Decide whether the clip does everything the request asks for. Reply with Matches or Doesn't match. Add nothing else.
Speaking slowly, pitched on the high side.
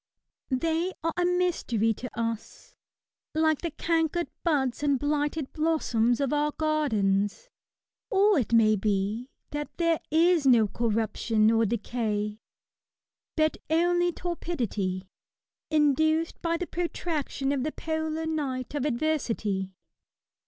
Matches